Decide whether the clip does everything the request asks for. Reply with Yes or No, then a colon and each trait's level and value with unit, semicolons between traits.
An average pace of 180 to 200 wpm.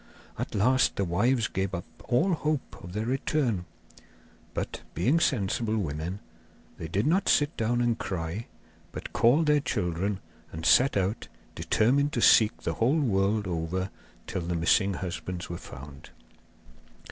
No: average, 145 wpm